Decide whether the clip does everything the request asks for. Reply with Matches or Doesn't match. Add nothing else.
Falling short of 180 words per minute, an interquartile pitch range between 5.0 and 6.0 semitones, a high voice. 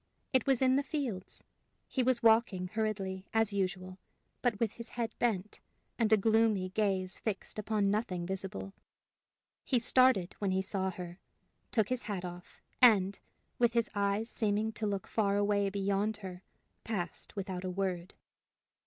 Doesn't match